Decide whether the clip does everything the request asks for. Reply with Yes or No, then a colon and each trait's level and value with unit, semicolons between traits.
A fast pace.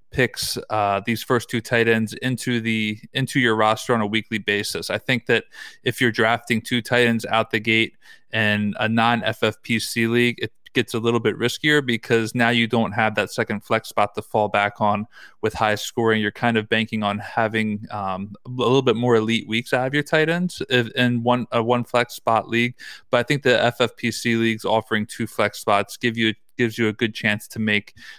Yes: fast, 210 wpm